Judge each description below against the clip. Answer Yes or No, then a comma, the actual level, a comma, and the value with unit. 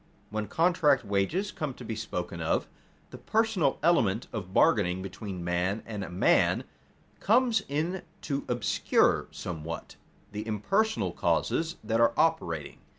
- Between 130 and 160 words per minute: Yes, slow, 135 wpm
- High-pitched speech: No, low, 115 Hz